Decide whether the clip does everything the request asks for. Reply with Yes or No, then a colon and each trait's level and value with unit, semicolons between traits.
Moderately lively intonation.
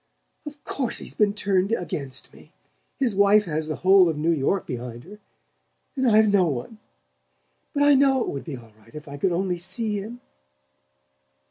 No: wide, 6.1 semitones